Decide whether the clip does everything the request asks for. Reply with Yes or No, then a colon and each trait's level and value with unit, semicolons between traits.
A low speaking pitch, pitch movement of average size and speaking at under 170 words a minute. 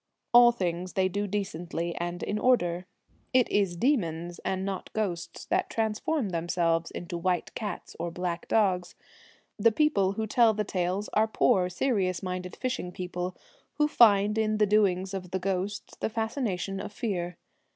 No: high, 190 Hz; average, 3.3 semitones; average, 160 wpm